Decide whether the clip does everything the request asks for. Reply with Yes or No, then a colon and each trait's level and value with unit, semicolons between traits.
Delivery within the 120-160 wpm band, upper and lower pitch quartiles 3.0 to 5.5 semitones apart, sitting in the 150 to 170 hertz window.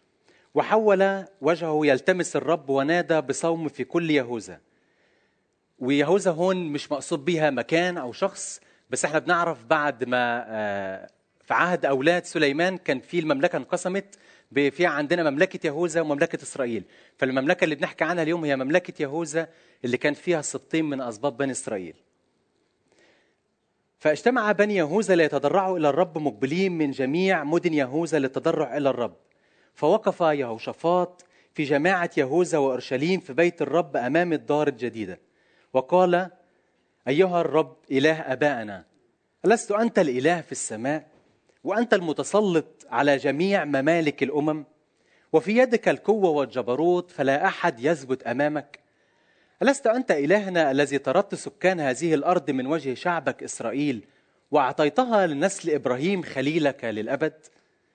Yes: average, 125 wpm; average, 4.2 semitones; medium, 160 Hz